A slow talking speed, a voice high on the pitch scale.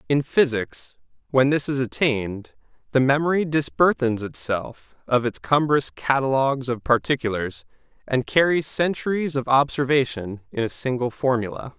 No: slow, 125 wpm; low, 130 Hz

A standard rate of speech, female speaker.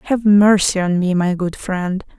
Yes: average, 195 wpm; female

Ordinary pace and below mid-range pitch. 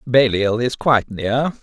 Yes: average, 150 wpm; low, 120 Hz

